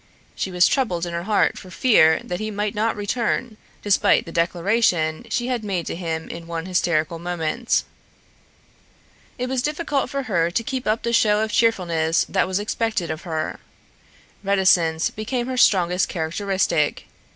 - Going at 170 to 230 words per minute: No, average, 160 wpm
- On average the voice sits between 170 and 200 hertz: Yes, high, 190 Hz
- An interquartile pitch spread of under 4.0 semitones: No, average, 5.2 semitones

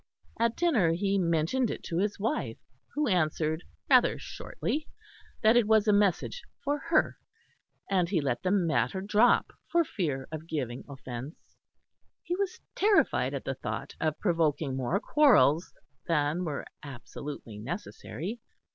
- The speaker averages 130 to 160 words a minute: Yes, average, 140 wpm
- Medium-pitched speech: Yes, medium, 180 Hz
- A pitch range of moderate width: No, wide, 6.5 semitones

